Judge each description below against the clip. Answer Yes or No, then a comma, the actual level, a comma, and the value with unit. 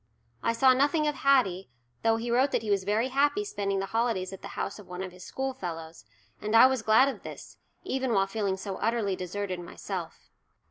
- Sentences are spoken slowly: No, fast, 205 wpm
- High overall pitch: Yes, high, 215 Hz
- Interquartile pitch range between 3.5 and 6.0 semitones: Yes, average, 5.2 semitones